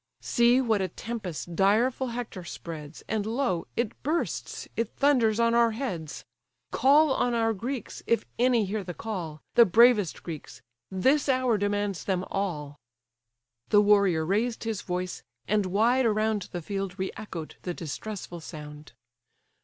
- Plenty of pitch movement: No, average, 4.7 semitones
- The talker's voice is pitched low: No, high, 210 Hz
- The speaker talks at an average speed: Yes, average, 145 wpm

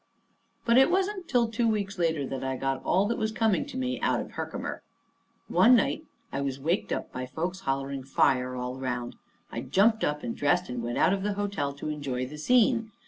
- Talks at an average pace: No, fast, 210 wpm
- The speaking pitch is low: No, medium, 165 Hz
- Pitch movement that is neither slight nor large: No, wide, 8.9 semitones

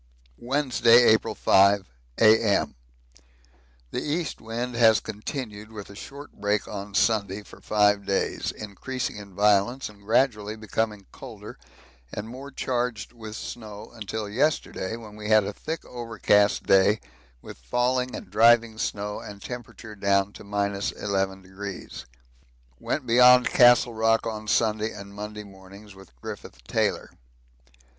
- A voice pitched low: Yes, low, 105 Hz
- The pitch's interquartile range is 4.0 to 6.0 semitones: No, average, 2.7 semitones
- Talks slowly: Yes, slow, 130 wpm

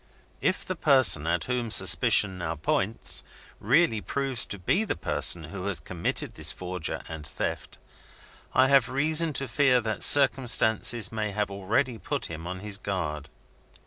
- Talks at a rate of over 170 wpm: No, average, 155 wpm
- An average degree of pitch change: No, wide, 6.5 semitones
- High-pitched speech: No, low, 105 Hz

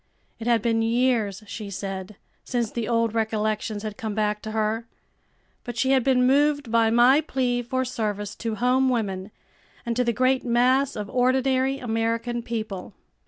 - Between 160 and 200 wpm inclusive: Yes, average, 165 wpm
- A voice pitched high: Yes, high, 230 Hz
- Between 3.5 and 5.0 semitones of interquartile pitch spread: No, average, 2.7 semitones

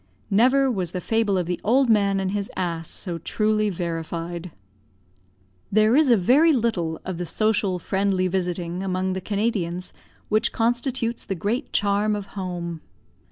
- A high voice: Yes, high, 195 Hz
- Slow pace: No, average, 155 wpm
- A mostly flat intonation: No, average, 3.8 semitones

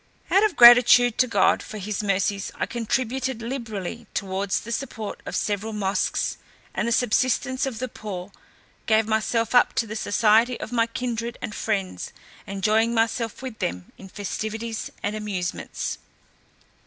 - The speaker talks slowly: No, average, 150 wpm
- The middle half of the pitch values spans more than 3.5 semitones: No, average, 2.7 semitones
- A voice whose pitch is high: Yes, high, 220 Hz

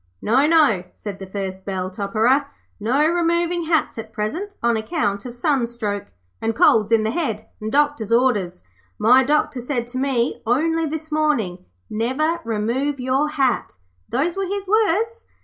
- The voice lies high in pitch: Yes, very high, 255 Hz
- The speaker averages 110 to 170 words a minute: Yes, average, 155 wpm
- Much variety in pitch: Yes, wide, 6.2 semitones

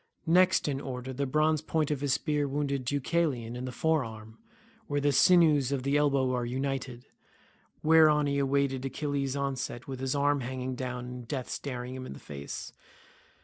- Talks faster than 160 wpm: Yes, average, 180 wpm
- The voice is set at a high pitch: No, low, 135 Hz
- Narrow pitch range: Yes, narrow, 2.3 semitones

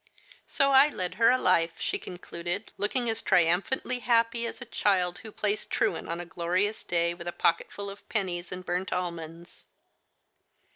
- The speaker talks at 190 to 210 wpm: No, average, 175 wpm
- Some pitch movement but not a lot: Yes, average, 4.4 semitones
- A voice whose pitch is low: No, medium, 185 Hz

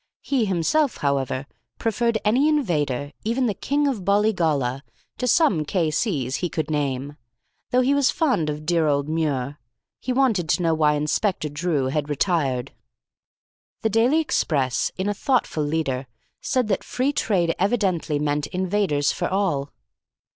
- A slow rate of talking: No, average, 145 wpm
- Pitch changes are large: Yes, wide, 7.3 semitones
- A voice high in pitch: No, medium, 170 Hz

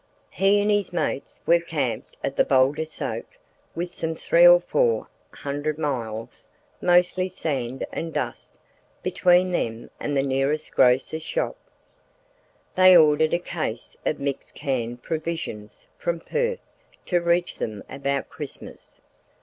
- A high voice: No, medium, 155 Hz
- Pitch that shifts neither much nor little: Yes, average, 4.6 semitones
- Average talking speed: No, slow, 125 wpm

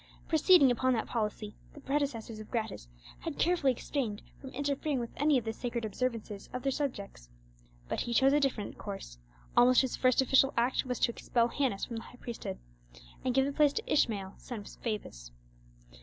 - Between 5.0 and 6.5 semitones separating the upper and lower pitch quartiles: No, average, 3.8 semitones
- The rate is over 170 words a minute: Yes, average, 185 wpm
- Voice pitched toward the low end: No, high, 245 Hz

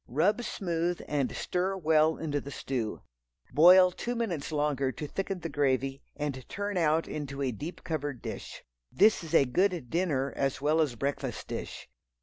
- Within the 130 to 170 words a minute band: Yes, average, 165 wpm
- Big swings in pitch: No, average, 4.4 semitones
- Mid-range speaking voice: Yes, medium, 155 Hz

